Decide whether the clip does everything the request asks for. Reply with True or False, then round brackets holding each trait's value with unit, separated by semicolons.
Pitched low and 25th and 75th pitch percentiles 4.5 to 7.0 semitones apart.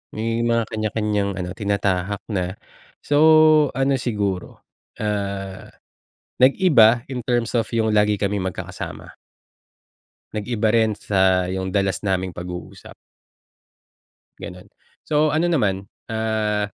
False (105 Hz; 3.4 semitones)